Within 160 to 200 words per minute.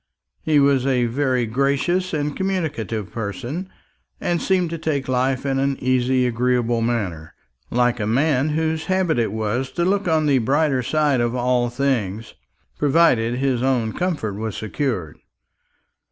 No: average, 150 wpm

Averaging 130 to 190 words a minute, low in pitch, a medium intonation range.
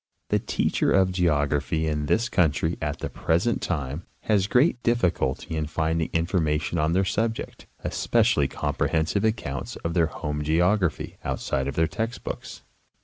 Yes: average, 145 wpm; very low, 80 Hz; average, 4.1 semitones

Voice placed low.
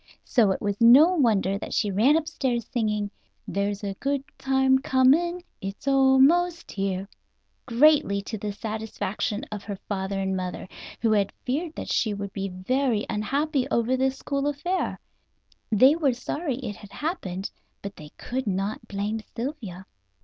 No: high, 230 Hz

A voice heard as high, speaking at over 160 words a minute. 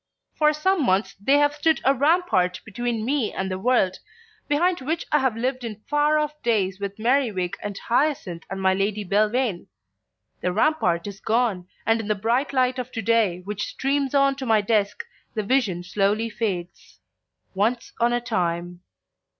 Yes: high, 225 Hz; average, 175 wpm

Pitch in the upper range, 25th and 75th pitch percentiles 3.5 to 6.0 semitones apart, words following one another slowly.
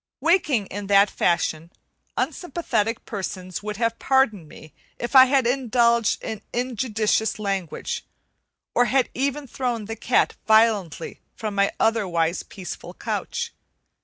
Yes: high, 225 Hz; average, 4.1 semitones; slow, 125 wpm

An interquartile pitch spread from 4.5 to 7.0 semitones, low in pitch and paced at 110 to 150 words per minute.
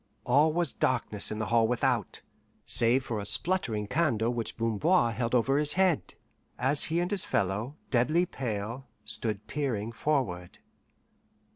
Yes: average, 5.3 semitones; low, 120 Hz; average, 145 wpm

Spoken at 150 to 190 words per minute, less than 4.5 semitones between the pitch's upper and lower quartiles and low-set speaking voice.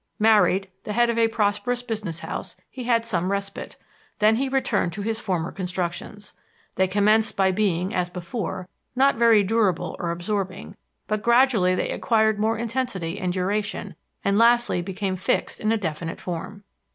No: average, 165 wpm; average, 3.5 semitones; high, 205 Hz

